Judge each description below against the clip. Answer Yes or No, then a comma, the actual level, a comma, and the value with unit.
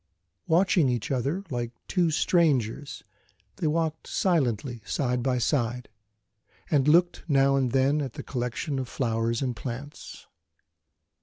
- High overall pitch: No, low, 135 Hz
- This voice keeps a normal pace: No, slow, 130 wpm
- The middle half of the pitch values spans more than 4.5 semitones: No, average, 3.9 semitones